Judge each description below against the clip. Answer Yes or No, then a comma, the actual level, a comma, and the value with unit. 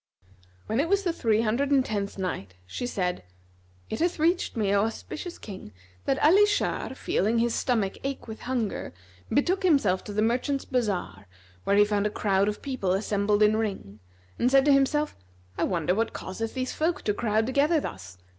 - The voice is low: No, high, 225 Hz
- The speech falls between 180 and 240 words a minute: Yes, average, 185 wpm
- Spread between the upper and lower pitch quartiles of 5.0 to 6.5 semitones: Yes, wide, 5.5 semitones